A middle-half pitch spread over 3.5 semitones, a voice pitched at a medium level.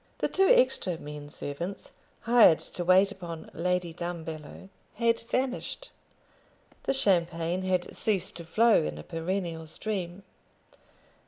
Yes: average, 3.9 semitones; medium, 180 Hz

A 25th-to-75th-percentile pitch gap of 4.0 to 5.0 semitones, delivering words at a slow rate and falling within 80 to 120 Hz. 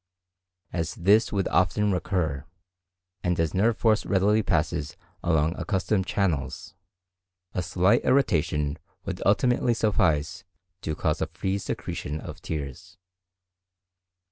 Yes: average, 4.5 semitones; slow, 115 wpm; very low, 90 Hz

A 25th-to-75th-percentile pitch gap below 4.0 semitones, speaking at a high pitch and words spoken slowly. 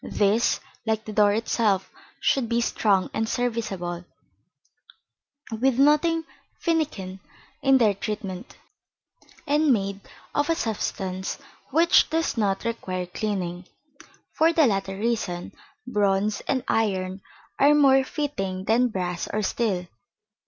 No: wide, 5.5 semitones; high, 215 Hz; slow, 115 wpm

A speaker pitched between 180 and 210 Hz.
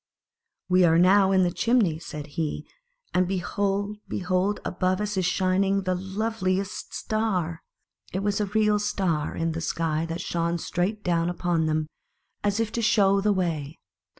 Yes: medium, 185 Hz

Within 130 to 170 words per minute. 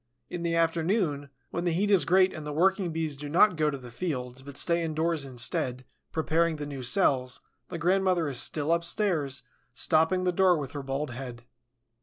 No: average, 190 wpm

